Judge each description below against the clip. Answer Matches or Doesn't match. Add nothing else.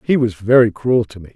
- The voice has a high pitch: Doesn't match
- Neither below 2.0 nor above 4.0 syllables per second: Doesn't match